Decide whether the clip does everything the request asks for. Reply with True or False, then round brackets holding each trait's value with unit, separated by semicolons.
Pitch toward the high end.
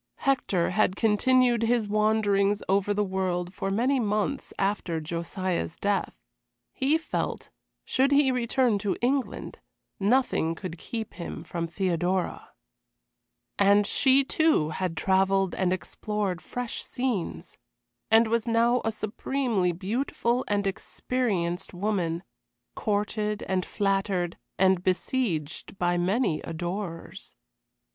True (200 Hz)